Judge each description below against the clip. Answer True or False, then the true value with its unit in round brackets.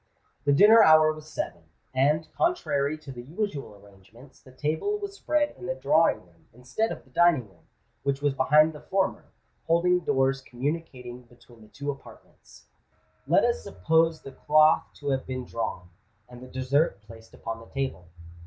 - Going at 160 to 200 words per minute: True (170 wpm)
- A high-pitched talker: False (140 Hz)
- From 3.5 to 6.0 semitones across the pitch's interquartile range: True (4.5 semitones)